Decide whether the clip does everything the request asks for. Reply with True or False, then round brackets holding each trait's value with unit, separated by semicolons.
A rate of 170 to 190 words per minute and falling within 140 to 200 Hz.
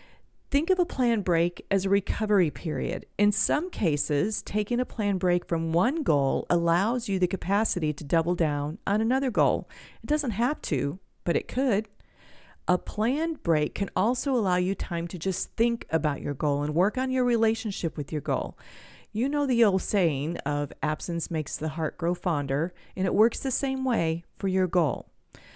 True (185 wpm; 185 Hz)